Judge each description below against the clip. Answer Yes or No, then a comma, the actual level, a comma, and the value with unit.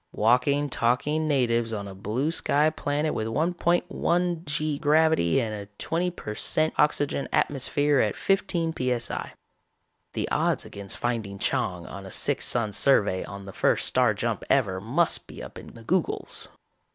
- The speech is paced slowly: No, average, 155 wpm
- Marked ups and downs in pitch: Yes, wide, 6.4 semitones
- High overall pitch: No, low, 130 Hz